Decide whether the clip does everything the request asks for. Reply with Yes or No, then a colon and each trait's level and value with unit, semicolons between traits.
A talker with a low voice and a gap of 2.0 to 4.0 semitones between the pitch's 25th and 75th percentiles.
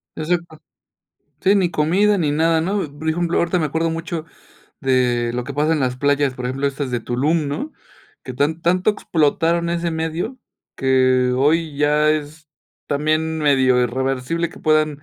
No: medium, 155 Hz; average, 3.6 semitones